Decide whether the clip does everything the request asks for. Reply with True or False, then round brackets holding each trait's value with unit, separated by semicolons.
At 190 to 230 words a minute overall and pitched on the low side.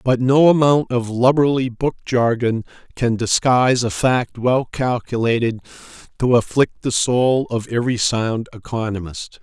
False (135 wpm; 120 Hz)